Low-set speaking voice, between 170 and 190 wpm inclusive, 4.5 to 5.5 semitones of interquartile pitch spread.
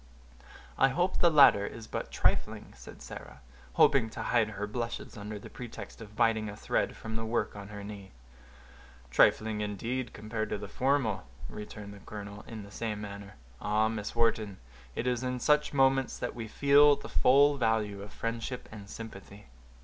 No: low, 110 Hz; average, 175 wpm; average, 3.1 semitones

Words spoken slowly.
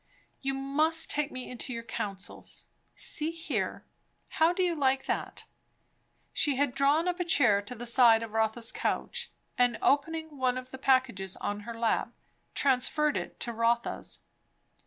No: average, 155 wpm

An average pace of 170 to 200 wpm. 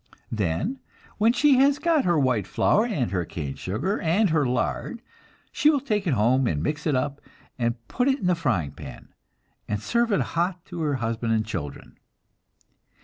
Yes: average, 185 wpm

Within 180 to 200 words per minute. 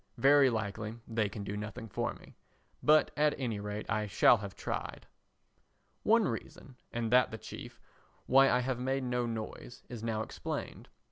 No: average, 165 wpm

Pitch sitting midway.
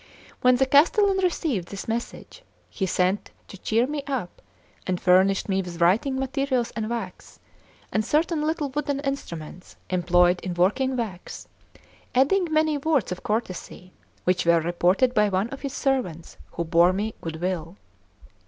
No: high, 215 Hz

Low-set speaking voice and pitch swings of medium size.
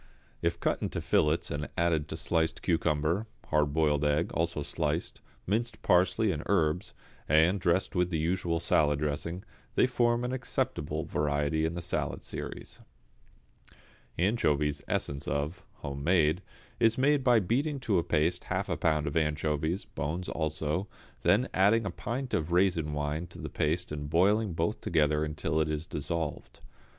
Yes: very low, 80 Hz; average, 3.8 semitones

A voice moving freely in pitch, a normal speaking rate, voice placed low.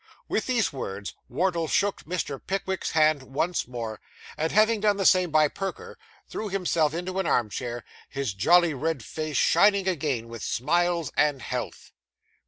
No: wide, 6.1 semitones; average, 160 wpm; medium, 160 Hz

